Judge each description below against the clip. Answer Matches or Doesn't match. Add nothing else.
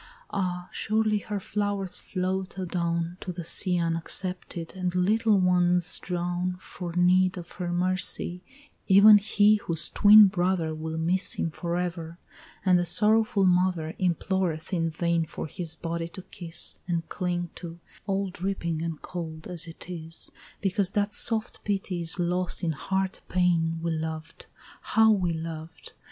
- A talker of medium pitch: Matches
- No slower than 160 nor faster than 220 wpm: Doesn't match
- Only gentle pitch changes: Matches